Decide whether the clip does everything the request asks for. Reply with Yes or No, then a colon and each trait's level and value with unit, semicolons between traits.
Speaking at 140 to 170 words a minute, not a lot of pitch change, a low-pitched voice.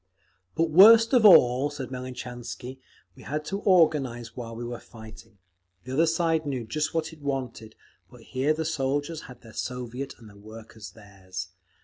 No: average, 165 wpm; average, 5.2 semitones; low, 130 Hz